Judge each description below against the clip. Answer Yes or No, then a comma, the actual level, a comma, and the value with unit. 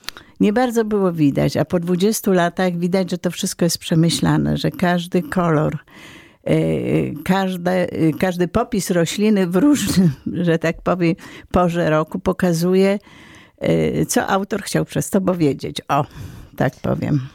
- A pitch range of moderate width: Yes, average, 3.3 semitones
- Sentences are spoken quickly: No, average, 140 wpm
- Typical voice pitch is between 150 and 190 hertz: Yes, medium, 180 Hz